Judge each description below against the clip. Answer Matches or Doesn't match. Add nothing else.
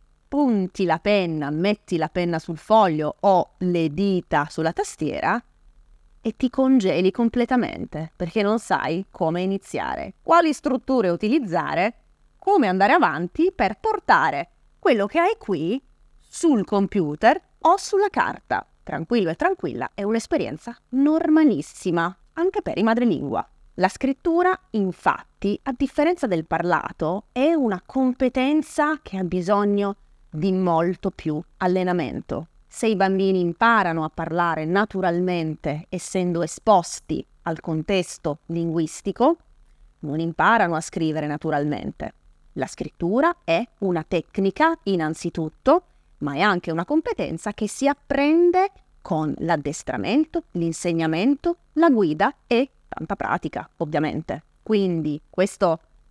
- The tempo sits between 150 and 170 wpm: Doesn't match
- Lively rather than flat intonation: Matches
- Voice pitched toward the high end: Matches